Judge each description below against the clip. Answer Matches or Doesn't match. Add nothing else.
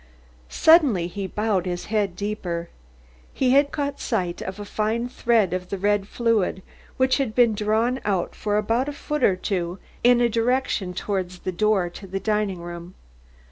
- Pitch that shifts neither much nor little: Matches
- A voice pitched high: Matches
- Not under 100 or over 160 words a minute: Doesn't match